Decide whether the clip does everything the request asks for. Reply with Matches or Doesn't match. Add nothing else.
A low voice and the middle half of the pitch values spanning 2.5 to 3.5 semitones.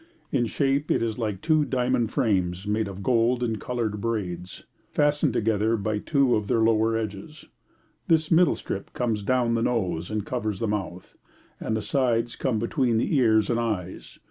Matches